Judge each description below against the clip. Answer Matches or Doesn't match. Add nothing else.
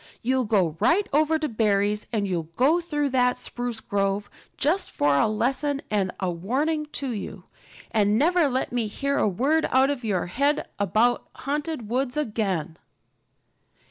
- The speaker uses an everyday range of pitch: Doesn't match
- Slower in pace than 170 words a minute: Matches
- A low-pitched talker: Doesn't match